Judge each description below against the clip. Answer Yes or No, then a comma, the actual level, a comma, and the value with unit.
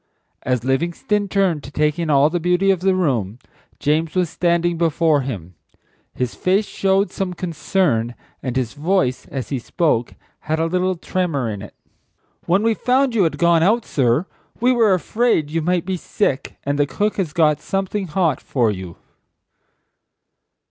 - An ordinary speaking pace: Yes, average, 170 wpm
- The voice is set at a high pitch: No, medium, 165 Hz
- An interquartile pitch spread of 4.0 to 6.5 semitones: Yes, average, 5.2 semitones